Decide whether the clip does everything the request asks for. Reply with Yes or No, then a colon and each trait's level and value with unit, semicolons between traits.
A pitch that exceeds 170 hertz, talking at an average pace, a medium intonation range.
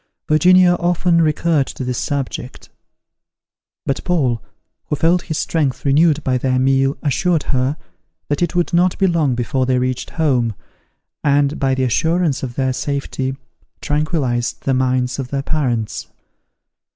No: medium, 140 Hz; average, 145 wpm; average, 4.0 semitones